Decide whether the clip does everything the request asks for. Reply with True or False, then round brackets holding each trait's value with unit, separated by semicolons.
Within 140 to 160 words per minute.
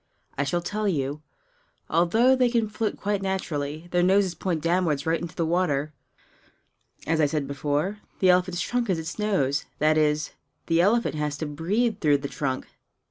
False (175 wpm)